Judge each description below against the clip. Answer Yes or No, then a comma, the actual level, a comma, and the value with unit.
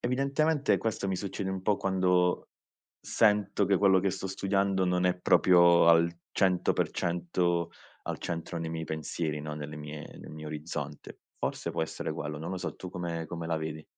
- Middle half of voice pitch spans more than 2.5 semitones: Yes, average, 2.9 semitones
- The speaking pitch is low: Yes, very low, 90 Hz